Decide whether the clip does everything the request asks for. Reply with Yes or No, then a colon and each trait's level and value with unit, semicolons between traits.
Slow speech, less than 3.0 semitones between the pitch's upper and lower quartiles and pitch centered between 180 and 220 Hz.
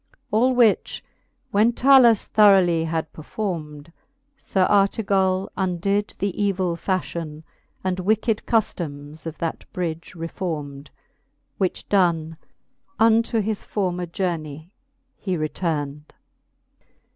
No: slow, 100 wpm; average, 4.1 semitones; medium, 185 Hz